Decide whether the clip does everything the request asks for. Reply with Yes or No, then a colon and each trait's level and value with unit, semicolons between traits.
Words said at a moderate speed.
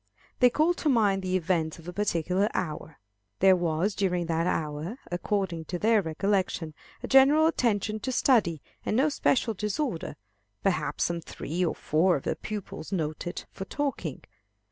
Yes: average, 160 wpm